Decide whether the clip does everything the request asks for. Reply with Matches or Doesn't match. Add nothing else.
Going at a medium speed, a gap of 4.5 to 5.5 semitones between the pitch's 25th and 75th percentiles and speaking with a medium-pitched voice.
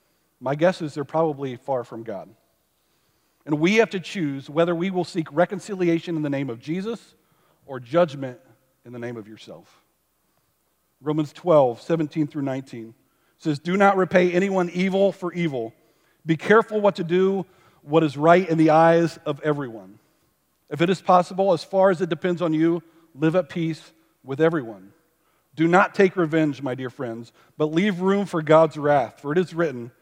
Doesn't match